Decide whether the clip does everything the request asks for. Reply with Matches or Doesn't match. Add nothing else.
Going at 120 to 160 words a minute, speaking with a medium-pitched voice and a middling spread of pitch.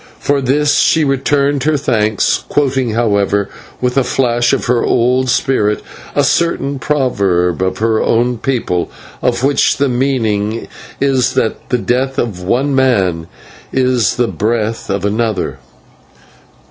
Doesn't match